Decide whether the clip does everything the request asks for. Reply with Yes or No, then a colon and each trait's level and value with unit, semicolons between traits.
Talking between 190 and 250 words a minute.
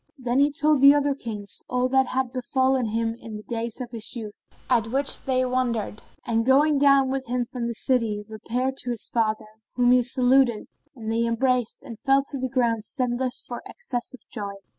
Yes: average, 200 wpm